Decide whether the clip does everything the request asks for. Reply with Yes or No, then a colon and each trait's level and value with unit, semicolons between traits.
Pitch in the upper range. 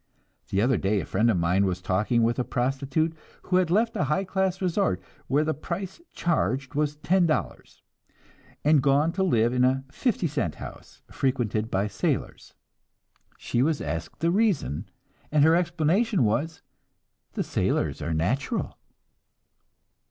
No: medium, 140 Hz